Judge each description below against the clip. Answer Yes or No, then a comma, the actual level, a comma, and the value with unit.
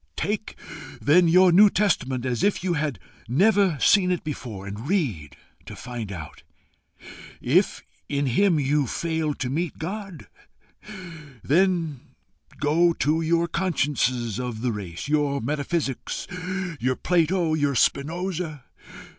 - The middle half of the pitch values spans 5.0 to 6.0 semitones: Yes, wide, 5.6 semitones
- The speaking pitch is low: No, medium, 150 Hz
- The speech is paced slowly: Yes, slow, 125 wpm